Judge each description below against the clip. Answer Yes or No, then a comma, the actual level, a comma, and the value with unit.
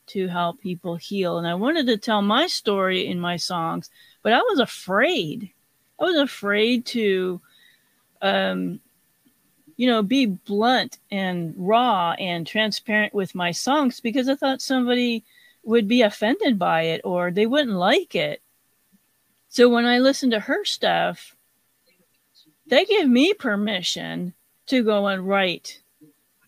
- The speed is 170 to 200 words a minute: No, average, 145 wpm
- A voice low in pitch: No, high, 215 Hz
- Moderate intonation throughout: No, wide, 5.8 semitones